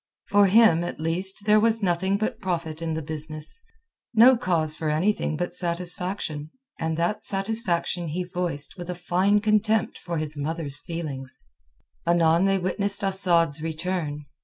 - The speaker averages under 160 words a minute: Yes, average, 150 wpm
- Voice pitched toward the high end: No, medium, 175 Hz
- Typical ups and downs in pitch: Yes, average, 3.6 semitones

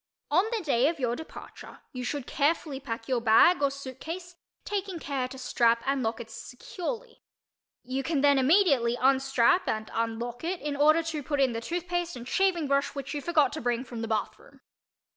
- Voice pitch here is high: Yes, very high, 275 Hz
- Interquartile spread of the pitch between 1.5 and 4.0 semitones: No, average, 5.2 semitones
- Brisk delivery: No, average, 195 wpm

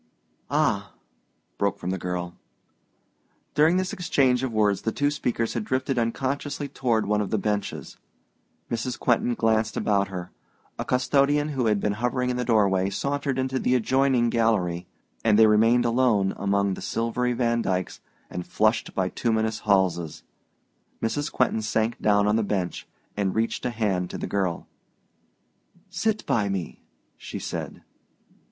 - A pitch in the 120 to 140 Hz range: No, low, 110 Hz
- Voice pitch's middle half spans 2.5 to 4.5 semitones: Yes, average, 4.0 semitones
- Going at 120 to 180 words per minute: Yes, average, 150 wpm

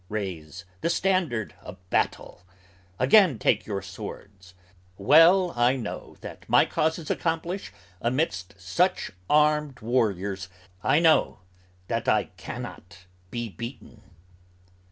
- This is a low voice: Yes, low, 120 Hz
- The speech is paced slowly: Yes, slow, 115 wpm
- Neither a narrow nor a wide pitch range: No, wide, 8.5 semitones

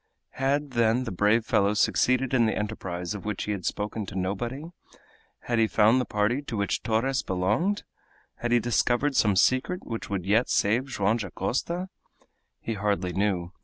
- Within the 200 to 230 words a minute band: No, average, 170 wpm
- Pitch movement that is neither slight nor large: Yes, average, 4.0 semitones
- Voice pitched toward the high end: No, low, 110 Hz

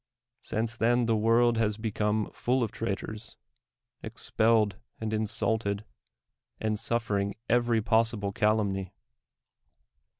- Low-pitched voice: Yes, low, 110 Hz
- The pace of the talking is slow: Yes, slow, 105 wpm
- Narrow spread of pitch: Yes, narrow, 1.6 semitones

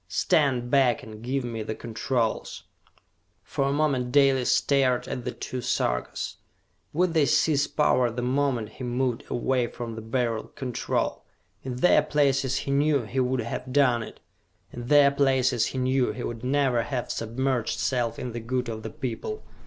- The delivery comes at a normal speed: Yes, average, 170 wpm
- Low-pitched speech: Yes, low, 125 Hz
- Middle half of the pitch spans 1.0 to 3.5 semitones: Yes, narrow, 2.6 semitones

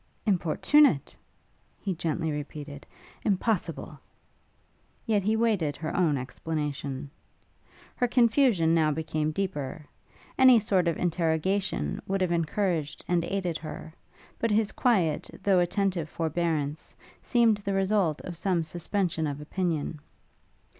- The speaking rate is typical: No, slow, 115 wpm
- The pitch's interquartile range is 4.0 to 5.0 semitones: Yes, average, 4.3 semitones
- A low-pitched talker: No, medium, 170 Hz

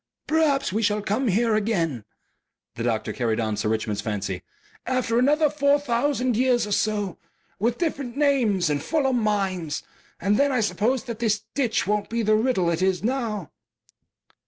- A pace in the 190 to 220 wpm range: No, average, 165 wpm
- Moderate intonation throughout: No, wide, 5.7 semitones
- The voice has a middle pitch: No, high, 215 Hz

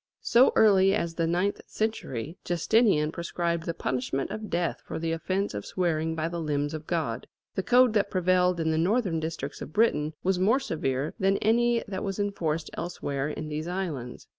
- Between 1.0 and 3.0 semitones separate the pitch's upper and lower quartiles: No, average, 4.1 semitones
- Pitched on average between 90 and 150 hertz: No, medium, 170 Hz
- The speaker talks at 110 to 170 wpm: No, average, 185 wpm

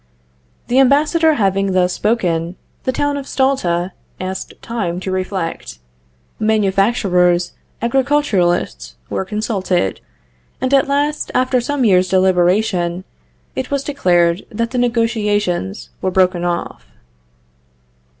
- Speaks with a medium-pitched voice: No, high, 195 Hz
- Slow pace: Yes, slow, 110 wpm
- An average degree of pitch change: No, wide, 6.0 semitones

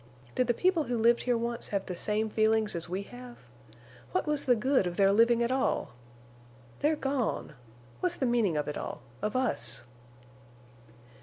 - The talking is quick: No, average, 170 wpm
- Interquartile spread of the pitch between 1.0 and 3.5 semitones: No, average, 4.2 semitones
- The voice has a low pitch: No, high, 230 Hz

